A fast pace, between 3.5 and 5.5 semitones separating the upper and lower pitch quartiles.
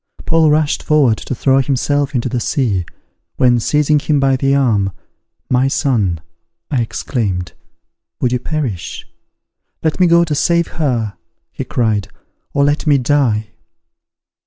No: average, 140 wpm; average, 4.3 semitones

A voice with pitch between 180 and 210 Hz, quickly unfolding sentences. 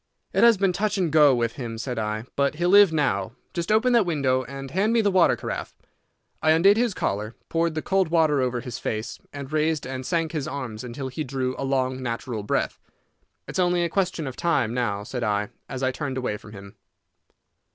No: medium, 140 Hz; fast, 215 wpm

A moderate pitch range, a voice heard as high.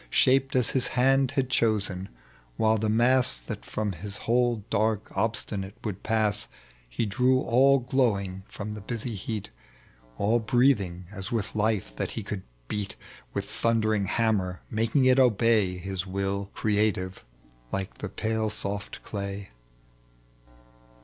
No: average, 3.1 semitones; low, 110 Hz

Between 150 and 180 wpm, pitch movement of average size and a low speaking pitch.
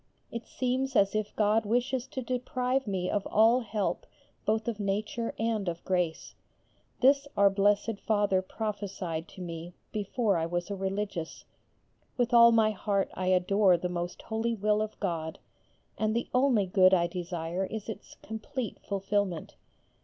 No: average, 155 wpm; average, 3.4 semitones; high, 205 Hz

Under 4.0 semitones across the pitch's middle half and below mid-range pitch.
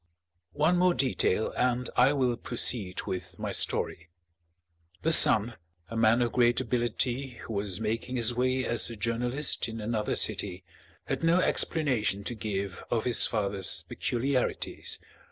Yes: average, 3.1 semitones; low, 120 Hz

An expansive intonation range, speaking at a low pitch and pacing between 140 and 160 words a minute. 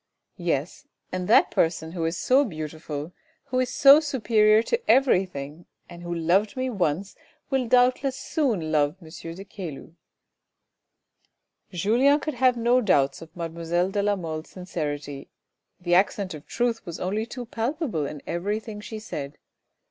No: wide, 6.5 semitones; medium, 185 Hz; average, 155 wpm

